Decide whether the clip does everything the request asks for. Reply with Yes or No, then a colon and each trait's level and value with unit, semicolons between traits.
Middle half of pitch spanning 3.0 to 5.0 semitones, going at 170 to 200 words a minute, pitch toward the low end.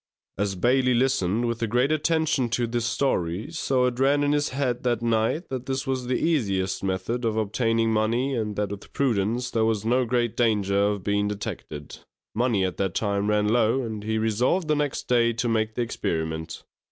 Yes: average, 3.6 semitones; average, 190 wpm; low, 115 Hz